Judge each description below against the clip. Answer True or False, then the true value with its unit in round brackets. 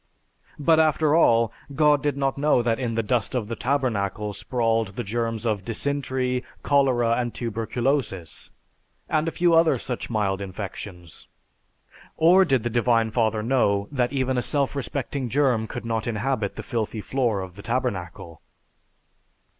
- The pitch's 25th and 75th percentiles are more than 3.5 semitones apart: True (4.0 semitones)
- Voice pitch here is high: False (120 Hz)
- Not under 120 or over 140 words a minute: False (155 wpm)